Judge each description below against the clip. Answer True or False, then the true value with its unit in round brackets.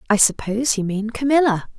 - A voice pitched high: True (230 Hz)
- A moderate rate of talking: True (170 wpm)